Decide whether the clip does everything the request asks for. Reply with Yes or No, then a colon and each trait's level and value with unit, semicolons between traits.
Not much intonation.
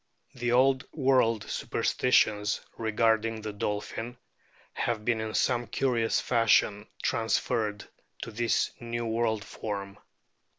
Yes: narrow, 2.0 semitones